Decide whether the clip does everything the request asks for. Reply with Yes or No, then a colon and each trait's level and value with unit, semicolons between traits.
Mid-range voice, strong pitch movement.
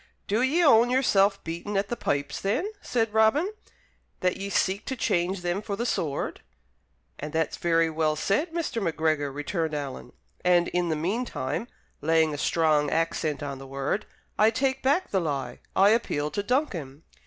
Yes: medium, 180 Hz; wide, 6.3 semitones